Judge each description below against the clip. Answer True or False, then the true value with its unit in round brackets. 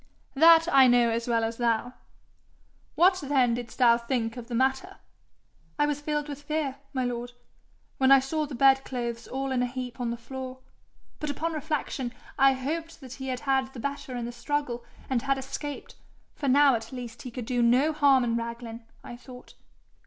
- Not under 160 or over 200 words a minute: True (190 wpm)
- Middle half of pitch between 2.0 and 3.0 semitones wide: True (2.7 semitones)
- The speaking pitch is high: True (260 Hz)